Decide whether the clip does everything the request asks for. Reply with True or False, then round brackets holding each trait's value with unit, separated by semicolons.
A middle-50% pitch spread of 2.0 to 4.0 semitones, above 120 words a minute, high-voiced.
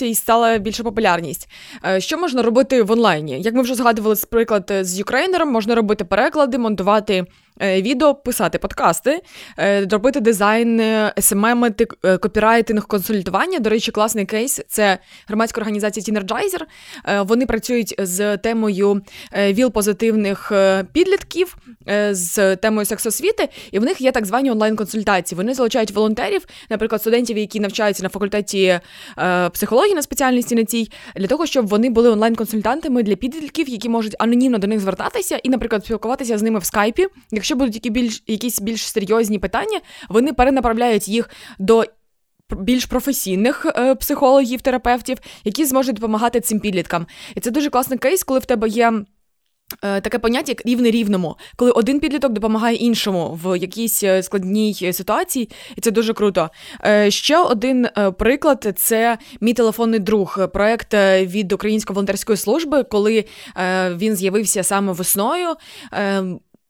True (3.3 semitones; 140 wpm; 225 Hz)